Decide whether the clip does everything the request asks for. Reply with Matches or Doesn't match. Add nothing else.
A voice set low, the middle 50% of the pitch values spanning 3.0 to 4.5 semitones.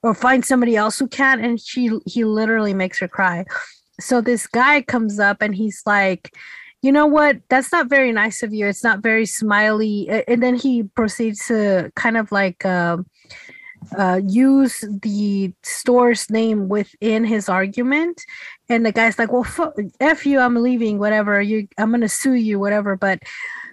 Doesn't match